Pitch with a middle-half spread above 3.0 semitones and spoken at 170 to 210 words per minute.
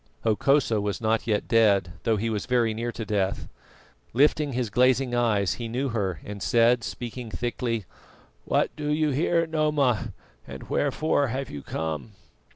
No: average, 4.1 semitones; average, 160 wpm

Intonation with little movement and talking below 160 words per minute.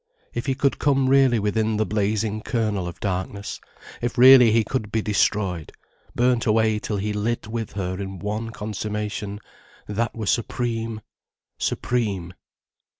Yes: narrow, 2.3 semitones; average, 145 wpm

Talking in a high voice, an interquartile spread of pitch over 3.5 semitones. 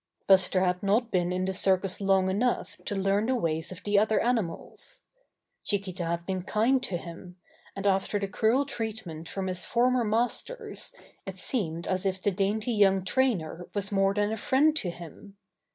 No: high, 195 Hz; average, 3.1 semitones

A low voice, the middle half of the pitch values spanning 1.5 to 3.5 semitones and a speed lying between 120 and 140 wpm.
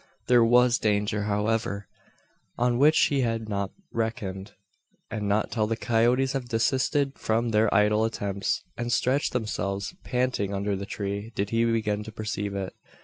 No: low, 110 Hz; average, 2.8 semitones; average, 155 wpm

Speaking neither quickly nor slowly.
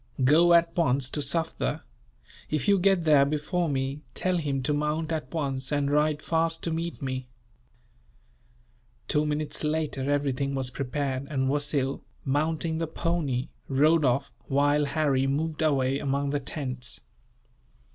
Yes: average, 145 wpm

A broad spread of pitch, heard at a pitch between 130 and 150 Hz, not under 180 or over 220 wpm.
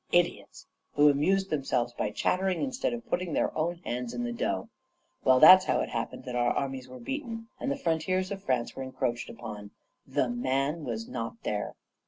Yes: wide, 7.4 semitones; medium, 140 Hz; average, 190 wpm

